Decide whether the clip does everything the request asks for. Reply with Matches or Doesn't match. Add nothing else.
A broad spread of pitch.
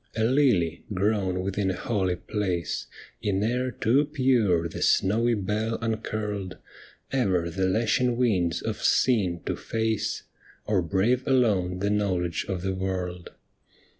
Doesn't match